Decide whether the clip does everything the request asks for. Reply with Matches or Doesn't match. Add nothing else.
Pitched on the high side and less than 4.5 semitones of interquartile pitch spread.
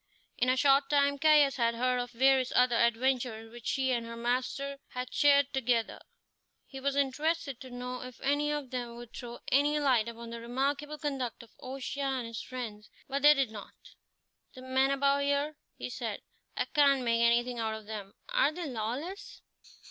Matches